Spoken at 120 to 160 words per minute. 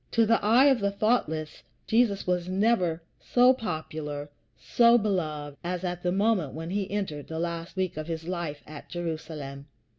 No: average, 170 wpm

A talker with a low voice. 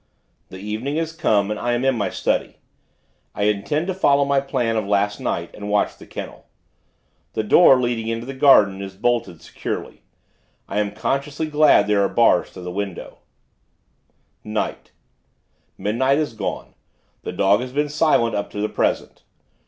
Yes: low, 115 Hz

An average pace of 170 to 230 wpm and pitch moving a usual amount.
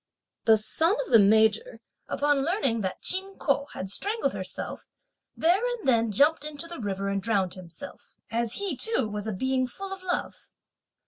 No: average, 175 wpm; wide, 8.9 semitones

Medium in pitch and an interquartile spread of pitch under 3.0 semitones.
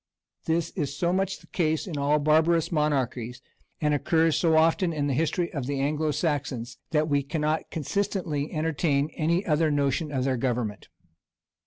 Yes: medium, 150 Hz; narrow, 2.5 semitones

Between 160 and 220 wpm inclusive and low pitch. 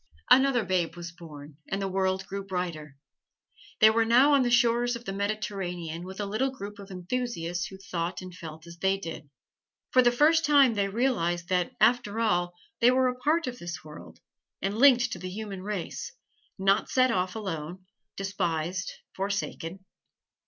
No: average, 175 wpm; high, 195 Hz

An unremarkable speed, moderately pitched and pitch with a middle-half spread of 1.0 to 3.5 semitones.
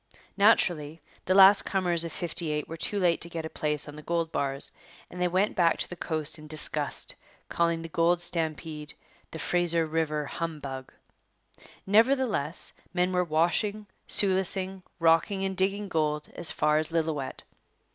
Yes: average, 155 wpm; medium, 170 Hz; average, 3.2 semitones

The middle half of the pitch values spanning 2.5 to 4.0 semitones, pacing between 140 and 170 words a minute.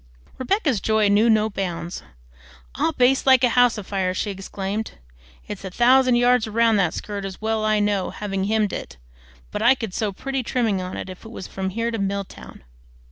No: average, 3.6 semitones; average, 190 wpm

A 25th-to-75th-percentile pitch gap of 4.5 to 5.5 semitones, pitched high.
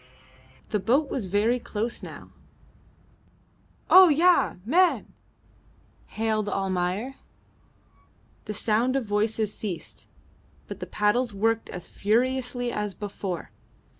No: average, 3.4 semitones; high, 220 Hz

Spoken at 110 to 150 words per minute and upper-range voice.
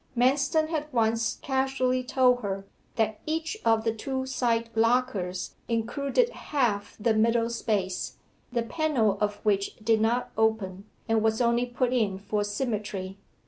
Yes: average, 140 wpm; high, 230 Hz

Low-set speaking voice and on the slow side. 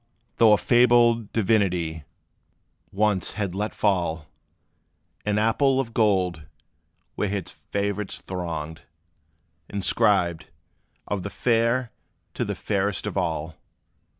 Yes: low, 100 Hz; slow, 105 wpm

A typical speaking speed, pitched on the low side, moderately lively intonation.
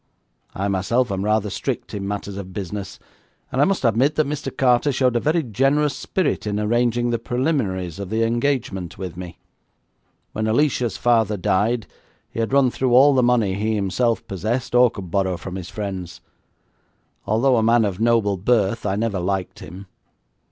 Yes: average, 175 wpm; low, 110 Hz; average, 4.0 semitones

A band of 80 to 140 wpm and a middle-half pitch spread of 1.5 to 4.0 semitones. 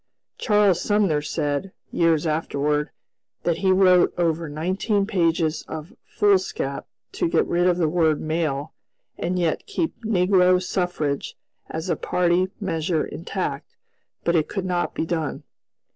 Yes: slow, 135 wpm; average, 2.9 semitones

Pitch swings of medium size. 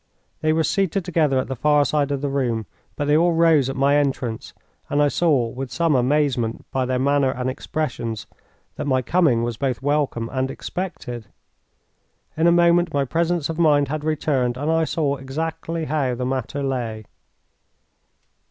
Yes: average, 3.5 semitones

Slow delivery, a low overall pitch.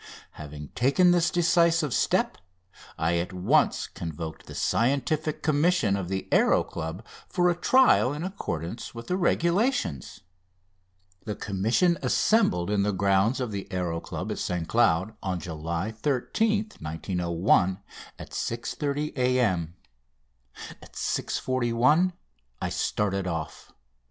Yes: slow, 120 wpm; low, 110 Hz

